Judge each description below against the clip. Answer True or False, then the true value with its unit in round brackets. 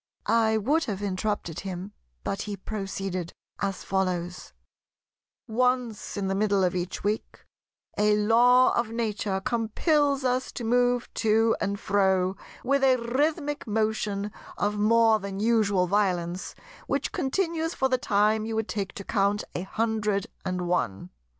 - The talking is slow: False (145 wpm)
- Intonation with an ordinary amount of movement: True (3.3 semitones)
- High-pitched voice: True (210 Hz)